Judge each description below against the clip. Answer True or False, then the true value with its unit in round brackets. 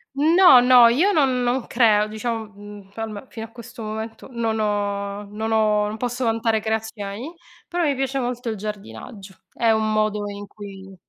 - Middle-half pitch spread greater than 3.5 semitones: False (2.7 semitones)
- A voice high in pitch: True (220 Hz)